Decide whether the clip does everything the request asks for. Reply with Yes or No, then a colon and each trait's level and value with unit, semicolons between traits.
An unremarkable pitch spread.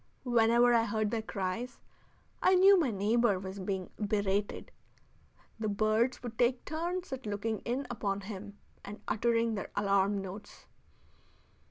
Yes: average, 3.1 semitones